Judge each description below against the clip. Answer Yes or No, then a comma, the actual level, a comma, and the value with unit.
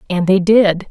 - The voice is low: No, high, 190 Hz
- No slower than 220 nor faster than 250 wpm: No, average, 200 wpm